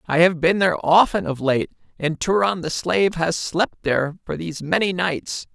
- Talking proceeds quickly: No, average, 195 wpm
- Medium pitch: Yes, medium, 170 Hz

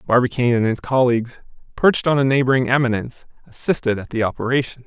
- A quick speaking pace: No, average, 160 wpm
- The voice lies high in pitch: No, low, 125 Hz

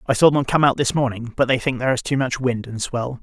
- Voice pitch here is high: No, low, 125 Hz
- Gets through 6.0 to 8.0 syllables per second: Yes, 6.2 syllables/s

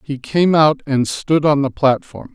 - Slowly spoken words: No, fast, 205 wpm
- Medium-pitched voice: Yes, medium, 145 Hz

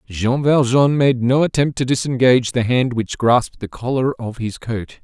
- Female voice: No, male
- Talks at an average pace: Yes, average, 190 wpm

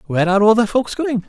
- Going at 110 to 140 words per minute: No, fast, 280 wpm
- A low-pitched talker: No, high, 215 Hz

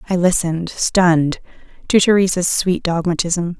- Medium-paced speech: No, slow, 115 wpm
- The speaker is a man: No, female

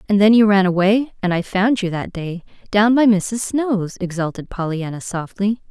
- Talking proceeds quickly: No, average, 190 wpm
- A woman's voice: Yes, female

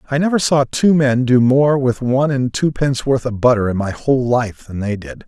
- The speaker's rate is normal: No, fast, 240 wpm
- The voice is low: Yes, low, 130 Hz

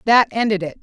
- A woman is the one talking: Yes, female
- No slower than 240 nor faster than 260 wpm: No, fast, 220 wpm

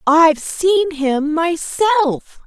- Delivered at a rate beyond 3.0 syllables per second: No, 2.6 syllables/s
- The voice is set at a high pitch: Yes, very high, 325 Hz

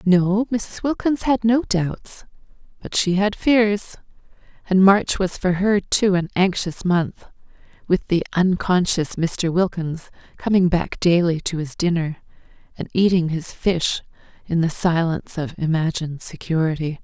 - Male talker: No, female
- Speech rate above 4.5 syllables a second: No, 4.2 syllables/s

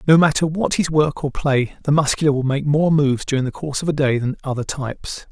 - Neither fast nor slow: No, fast, 250 wpm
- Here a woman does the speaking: No, male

